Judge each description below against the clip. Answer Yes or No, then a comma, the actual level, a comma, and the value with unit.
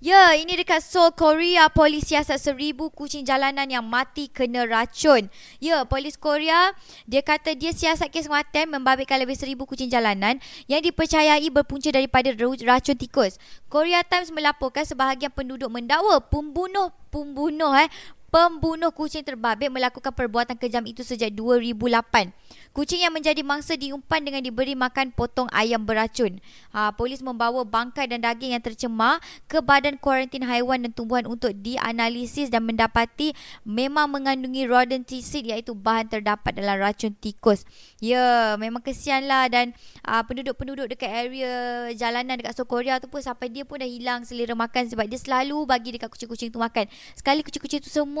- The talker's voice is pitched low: No, very high, 265 Hz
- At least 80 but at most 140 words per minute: No, fast, 155 wpm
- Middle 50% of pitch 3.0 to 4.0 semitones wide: Yes, average, 3.6 semitones